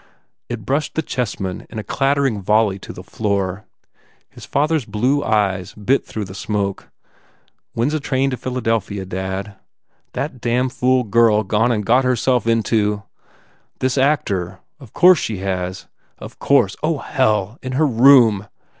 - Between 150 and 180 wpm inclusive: Yes, average, 155 wpm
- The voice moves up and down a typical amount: Yes, average, 4.4 semitones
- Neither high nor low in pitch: No, low, 115 Hz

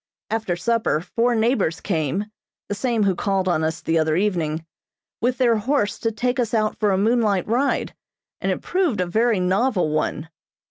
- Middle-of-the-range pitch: No, high, 210 Hz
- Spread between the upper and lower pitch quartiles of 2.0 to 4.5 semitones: No, average, 5.0 semitones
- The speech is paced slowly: No, average, 180 wpm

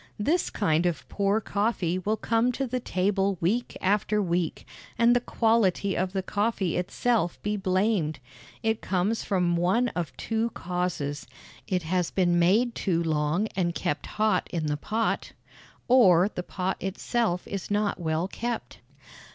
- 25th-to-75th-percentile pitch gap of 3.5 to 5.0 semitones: Yes, average, 4.0 semitones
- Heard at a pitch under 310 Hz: Yes, high, 190 Hz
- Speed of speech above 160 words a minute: No, average, 150 wpm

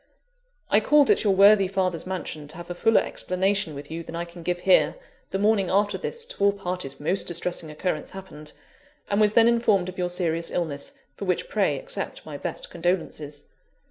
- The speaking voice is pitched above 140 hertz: Yes, medium, 185 Hz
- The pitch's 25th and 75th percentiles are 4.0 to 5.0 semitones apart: No, average, 3.2 semitones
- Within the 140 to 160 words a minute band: No, average, 195 wpm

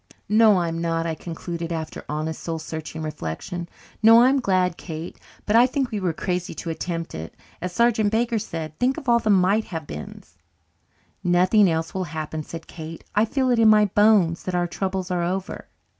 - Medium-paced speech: Yes, average, 190 wpm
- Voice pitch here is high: No, medium, 180 Hz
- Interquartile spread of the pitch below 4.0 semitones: No, average, 4.6 semitones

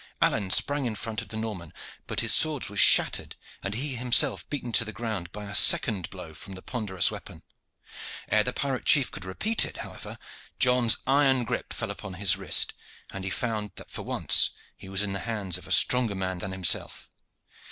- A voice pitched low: Yes, low, 110 Hz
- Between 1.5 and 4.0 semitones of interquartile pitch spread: No, average, 4.7 semitones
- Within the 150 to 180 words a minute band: No, average, 200 wpm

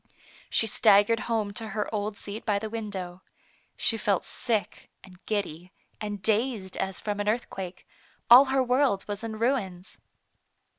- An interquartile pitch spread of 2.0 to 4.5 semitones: Yes, narrow, 2.5 semitones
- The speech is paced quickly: No, average, 150 wpm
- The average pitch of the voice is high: Yes, high, 210 Hz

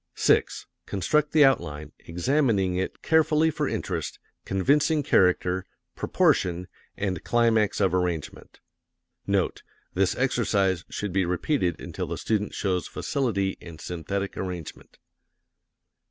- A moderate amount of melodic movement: No, wide, 5.9 semitones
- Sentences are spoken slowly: Yes, slow, 110 wpm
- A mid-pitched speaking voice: No, very low, 95 Hz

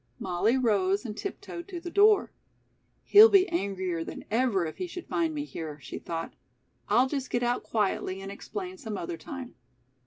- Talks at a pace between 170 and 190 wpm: Yes, average, 180 wpm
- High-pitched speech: Yes, high, 240 Hz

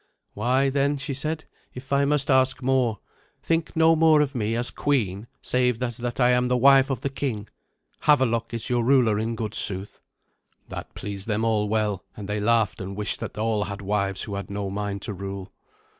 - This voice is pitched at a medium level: No, low, 115 Hz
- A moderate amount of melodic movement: Yes, average, 4.4 semitones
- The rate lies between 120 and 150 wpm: No, average, 200 wpm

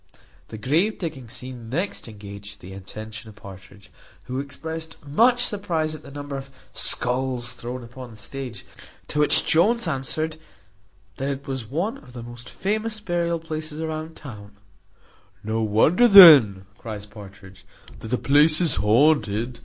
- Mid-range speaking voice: No, low, 130 Hz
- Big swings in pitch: Yes, wide, 6.4 semitones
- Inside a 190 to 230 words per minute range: No, average, 150 wpm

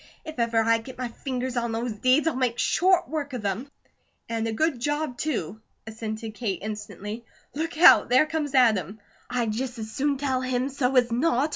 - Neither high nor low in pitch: No, high, 245 Hz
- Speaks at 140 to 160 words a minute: No, average, 190 wpm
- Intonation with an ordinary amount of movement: Yes, average, 3.8 semitones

